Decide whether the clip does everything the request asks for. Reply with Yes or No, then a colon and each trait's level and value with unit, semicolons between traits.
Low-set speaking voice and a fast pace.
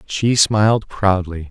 No: low, 100 Hz; slow, 120 wpm